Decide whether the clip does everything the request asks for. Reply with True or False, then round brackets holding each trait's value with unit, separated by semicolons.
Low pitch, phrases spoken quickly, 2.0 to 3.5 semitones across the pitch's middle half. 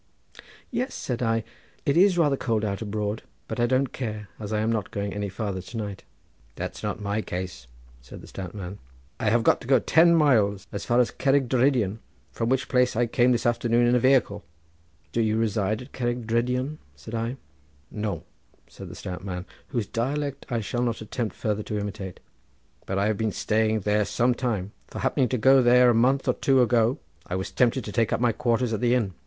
True (115 Hz; 210 wpm; 3.2 semitones)